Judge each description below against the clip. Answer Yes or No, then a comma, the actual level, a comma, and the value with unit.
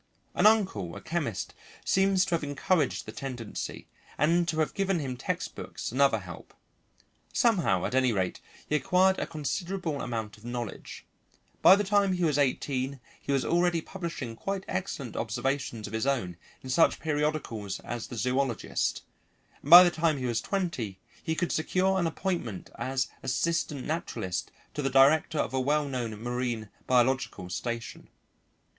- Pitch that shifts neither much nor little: No, wide, 6.1 semitones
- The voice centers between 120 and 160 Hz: Yes, medium, 140 Hz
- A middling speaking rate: Yes, average, 160 wpm